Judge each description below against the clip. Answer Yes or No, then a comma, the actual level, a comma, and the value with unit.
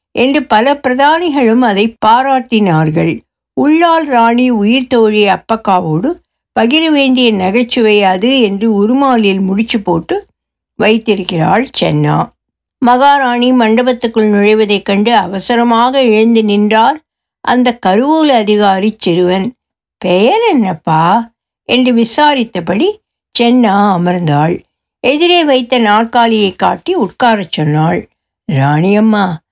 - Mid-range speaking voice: No, high, 230 Hz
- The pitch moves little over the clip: No, average, 4.4 semitones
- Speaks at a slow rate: No, average, 90 wpm